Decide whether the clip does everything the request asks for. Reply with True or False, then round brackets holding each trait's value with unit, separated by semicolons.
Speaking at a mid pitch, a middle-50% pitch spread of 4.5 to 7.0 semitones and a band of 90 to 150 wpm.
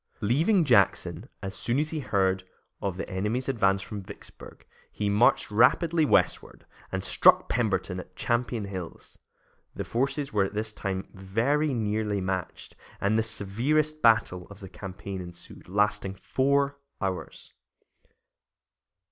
False (105 Hz; 4.8 semitones; 135 wpm)